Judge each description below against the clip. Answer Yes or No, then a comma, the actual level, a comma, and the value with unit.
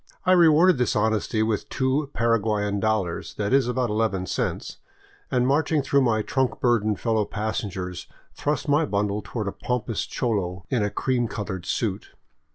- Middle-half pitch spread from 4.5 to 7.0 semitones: No, average, 4.0 semitones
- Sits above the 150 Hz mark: No, low, 110 Hz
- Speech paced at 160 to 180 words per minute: Yes, average, 170 wpm